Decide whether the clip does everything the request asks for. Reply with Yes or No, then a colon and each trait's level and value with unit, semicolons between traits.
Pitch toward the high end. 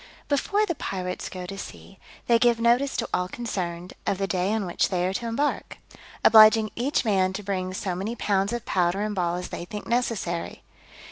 Yes: high, 200 Hz